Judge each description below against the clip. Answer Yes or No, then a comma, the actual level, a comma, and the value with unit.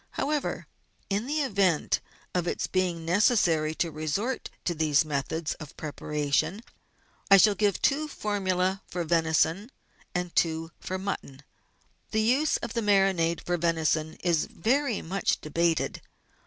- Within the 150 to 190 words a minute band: No, average, 140 wpm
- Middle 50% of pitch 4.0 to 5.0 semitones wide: Yes, average, 4.3 semitones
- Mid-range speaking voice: Yes, medium, 180 Hz